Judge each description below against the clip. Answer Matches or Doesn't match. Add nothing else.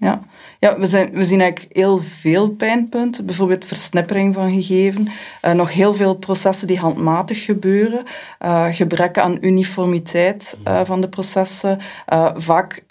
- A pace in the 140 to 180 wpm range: Matches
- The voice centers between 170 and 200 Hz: Matches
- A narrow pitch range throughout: Matches